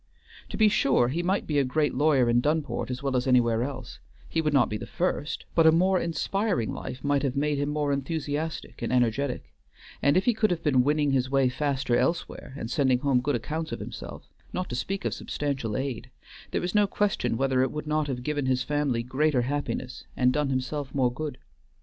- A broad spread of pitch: No, average, 3.4 semitones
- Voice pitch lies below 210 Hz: Yes, medium, 140 Hz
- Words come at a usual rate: No, fast, 215 wpm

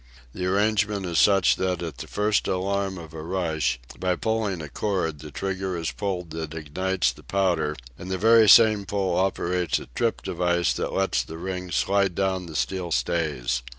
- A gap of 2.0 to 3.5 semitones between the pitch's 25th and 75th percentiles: Yes, average, 3.1 semitones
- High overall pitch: No, very low, 90 Hz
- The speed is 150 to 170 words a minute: No, average, 185 wpm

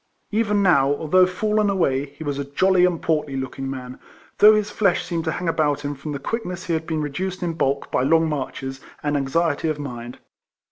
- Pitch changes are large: No, average, 4.6 semitones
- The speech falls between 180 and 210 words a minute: Yes, fast, 205 wpm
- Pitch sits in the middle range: Yes, medium, 155 Hz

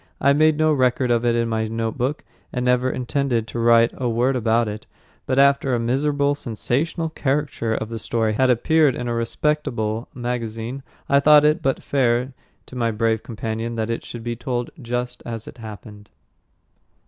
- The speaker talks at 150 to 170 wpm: No, average, 180 wpm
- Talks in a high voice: No, low, 120 Hz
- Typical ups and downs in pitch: Yes, average, 3.0 semitones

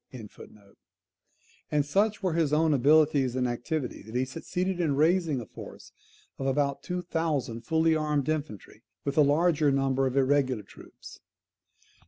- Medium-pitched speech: Yes, medium, 145 Hz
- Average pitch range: Yes, average, 3.4 semitones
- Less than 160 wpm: Yes, average, 150 wpm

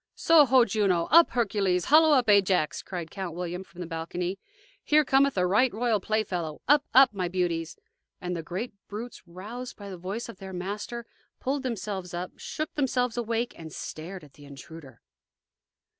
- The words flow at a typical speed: Yes, average, 170 wpm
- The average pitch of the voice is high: Yes, high, 195 Hz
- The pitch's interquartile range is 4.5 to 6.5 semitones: Yes, wide, 5.4 semitones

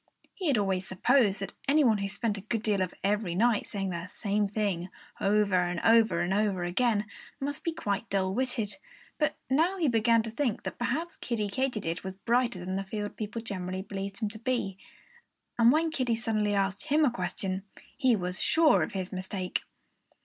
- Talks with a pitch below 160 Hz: No, high, 210 Hz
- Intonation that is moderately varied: Yes, average, 3.9 semitones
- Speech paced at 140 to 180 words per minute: No, average, 195 wpm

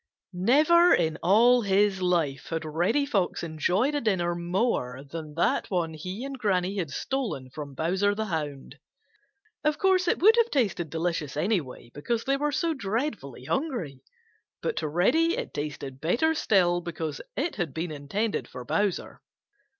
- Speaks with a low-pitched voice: No, medium, 180 Hz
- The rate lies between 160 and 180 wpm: Yes, average, 165 wpm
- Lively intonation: Yes, wide, 7.5 semitones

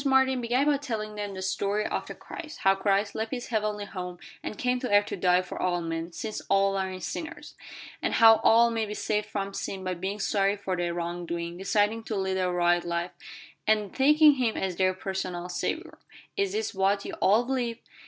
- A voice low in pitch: No, high, 200 Hz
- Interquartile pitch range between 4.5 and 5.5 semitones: No, average, 3.5 semitones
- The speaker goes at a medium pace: No, fast, 210 wpm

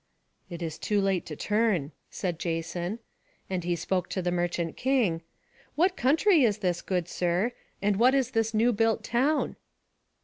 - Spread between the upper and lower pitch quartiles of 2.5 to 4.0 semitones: No, average, 5.3 semitones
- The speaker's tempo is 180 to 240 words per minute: No, average, 165 wpm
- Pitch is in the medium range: No, high, 195 Hz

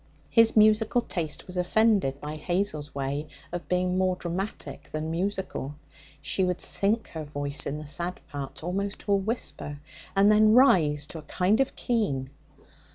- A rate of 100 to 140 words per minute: No, average, 160 wpm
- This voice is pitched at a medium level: Yes, medium, 180 Hz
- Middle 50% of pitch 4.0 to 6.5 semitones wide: Yes, wide, 5.5 semitones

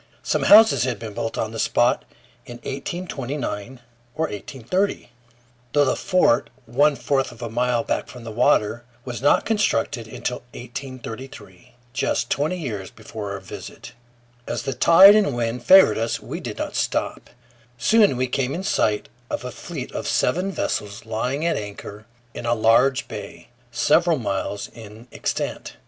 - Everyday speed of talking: Yes, average, 155 wpm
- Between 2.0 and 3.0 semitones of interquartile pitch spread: No, average, 4.3 semitones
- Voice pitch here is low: Yes, low, 125 Hz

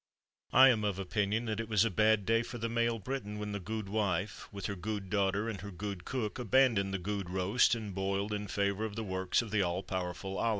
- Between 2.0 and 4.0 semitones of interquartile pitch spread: Yes, narrow, 2.4 semitones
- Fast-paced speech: Yes, fast, 230 wpm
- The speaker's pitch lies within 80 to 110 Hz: Yes, low, 105 Hz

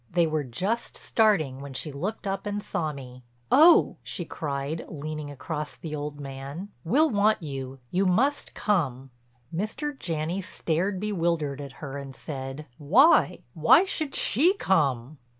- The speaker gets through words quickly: No, average, 140 wpm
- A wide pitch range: Yes, wide, 6.5 semitones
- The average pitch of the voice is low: No, medium, 160 Hz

